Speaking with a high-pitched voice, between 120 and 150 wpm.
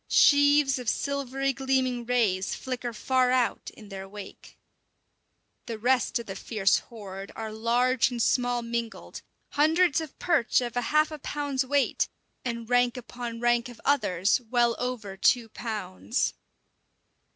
Yes: high, 245 Hz; average, 140 wpm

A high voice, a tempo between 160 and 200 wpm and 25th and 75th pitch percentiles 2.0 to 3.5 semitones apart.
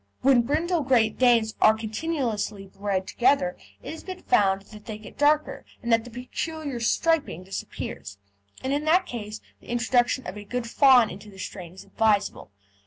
No: high, 235 Hz; average, 175 wpm; average, 4.9 semitones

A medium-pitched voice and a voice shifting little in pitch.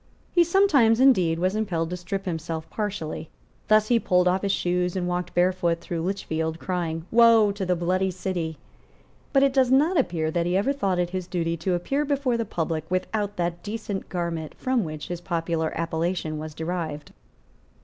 No: medium, 180 Hz; average, 4.2 semitones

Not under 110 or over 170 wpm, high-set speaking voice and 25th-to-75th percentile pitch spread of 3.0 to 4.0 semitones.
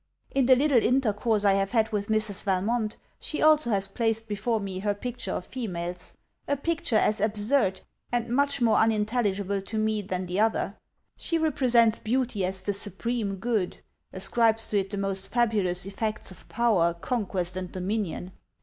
Yes: average, 165 wpm; high, 215 Hz; average, 3.5 semitones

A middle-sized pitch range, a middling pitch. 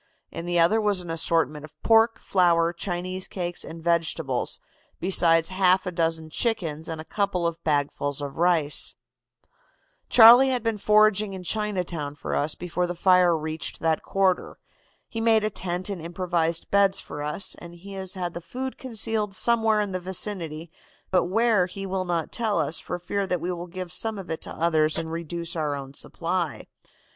Yes: average, 3.3 semitones; medium, 175 Hz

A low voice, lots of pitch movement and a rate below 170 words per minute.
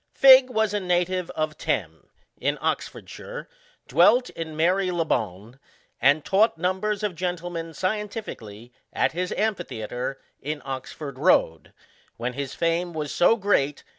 No: medium, 170 Hz; wide, 5.9 semitones; slow, 135 wpm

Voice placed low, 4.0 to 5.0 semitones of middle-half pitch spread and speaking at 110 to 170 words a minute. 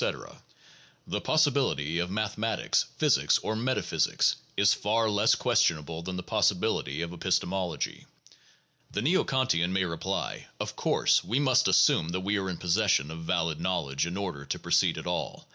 Yes: very low, 95 Hz; average, 4.6 semitones; average, 155 wpm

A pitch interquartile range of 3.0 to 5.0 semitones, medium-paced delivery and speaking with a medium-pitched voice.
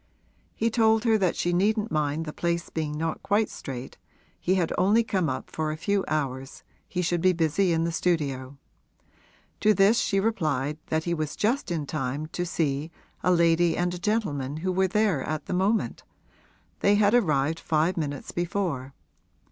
Yes: average, 4.4 semitones; average, 180 wpm; medium, 170 Hz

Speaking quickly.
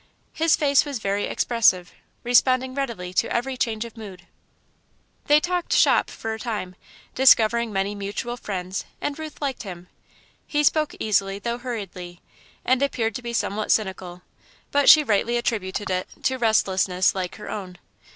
No: average, 155 wpm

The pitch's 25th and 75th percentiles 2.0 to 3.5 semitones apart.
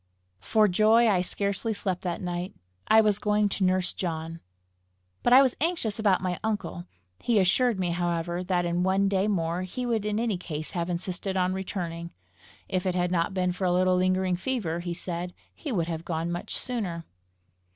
Yes: average, 3.1 semitones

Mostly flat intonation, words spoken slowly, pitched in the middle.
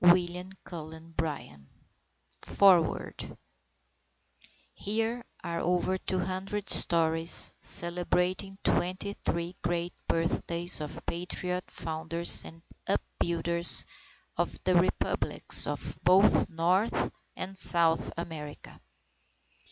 Yes: narrow, 2.0 semitones; slow, 85 wpm; medium, 175 Hz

